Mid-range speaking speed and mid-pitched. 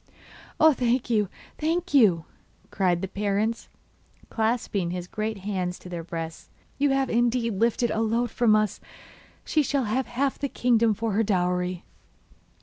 No: average, 150 wpm; high, 220 Hz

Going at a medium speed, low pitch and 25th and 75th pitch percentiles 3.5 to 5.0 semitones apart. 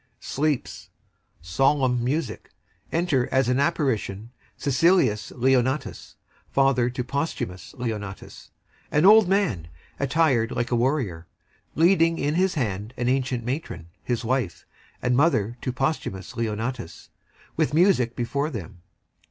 No: slow, 115 wpm; low, 130 Hz; average, 4.4 semitones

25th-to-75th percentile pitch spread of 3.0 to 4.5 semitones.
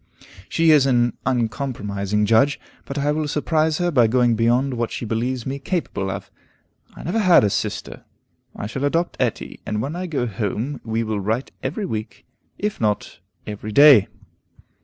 No: average, 5.3 semitones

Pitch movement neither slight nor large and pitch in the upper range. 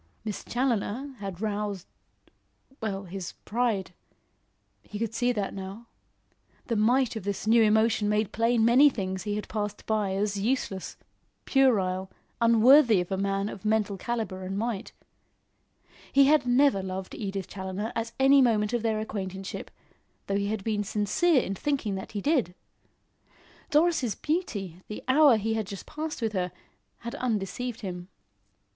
Yes: average, 3.5 semitones; high, 215 Hz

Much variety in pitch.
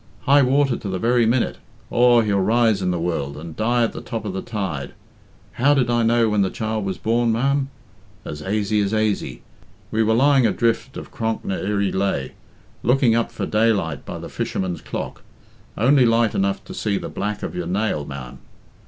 No: average, 3.7 semitones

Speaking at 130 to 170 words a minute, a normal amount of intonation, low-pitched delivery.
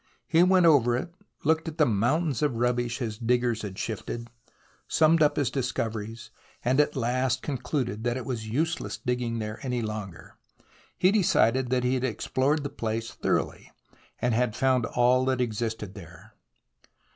Yes: average, 160 wpm; average, 3.4 semitones; low, 125 Hz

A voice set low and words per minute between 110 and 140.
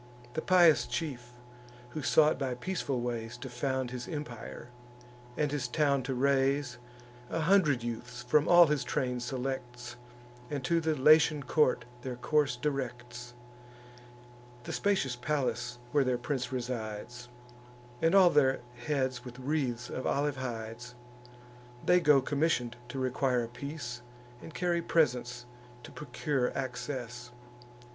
Yes: low, 130 Hz; slow, 135 wpm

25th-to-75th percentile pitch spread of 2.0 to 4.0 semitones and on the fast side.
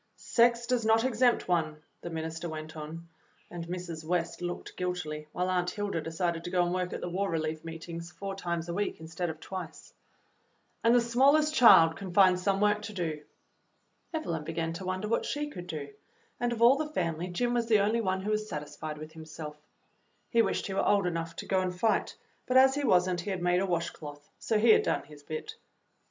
No: average, 4.5 semitones; fast, 220 wpm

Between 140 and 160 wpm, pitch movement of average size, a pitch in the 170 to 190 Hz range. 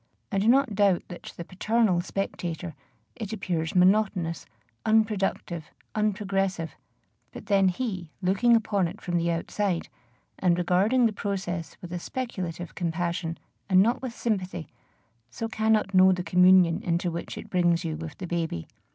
Yes: average, 150 wpm; average, 3.4 semitones; medium, 185 Hz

